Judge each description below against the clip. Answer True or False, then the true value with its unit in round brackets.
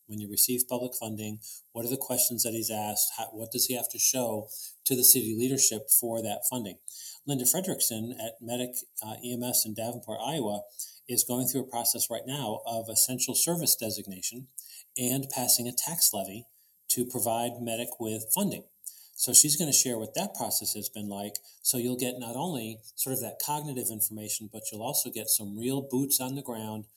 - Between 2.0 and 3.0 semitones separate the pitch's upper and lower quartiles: True (2.5 semitones)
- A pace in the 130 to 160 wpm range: False (195 wpm)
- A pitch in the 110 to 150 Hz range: True (120 Hz)